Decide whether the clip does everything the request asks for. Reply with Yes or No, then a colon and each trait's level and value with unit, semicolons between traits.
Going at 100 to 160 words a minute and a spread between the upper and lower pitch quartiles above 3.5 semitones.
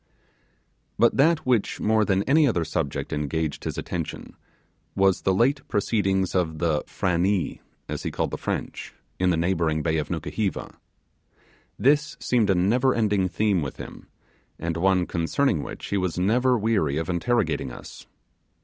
Yes: average, 155 wpm; average, 5.2 semitones